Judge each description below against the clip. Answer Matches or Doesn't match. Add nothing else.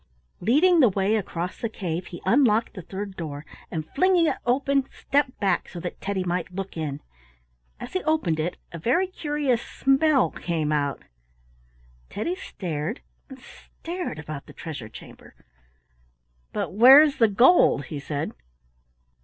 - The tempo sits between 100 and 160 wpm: Matches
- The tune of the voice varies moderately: Doesn't match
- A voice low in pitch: Doesn't match